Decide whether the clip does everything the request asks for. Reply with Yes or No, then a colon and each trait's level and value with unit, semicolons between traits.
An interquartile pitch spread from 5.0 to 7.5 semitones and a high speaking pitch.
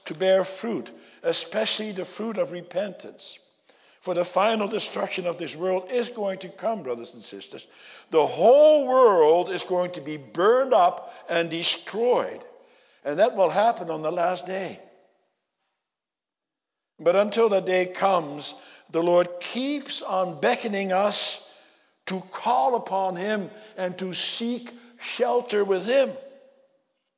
Yes: average, 5.3 semitones; high, 195 Hz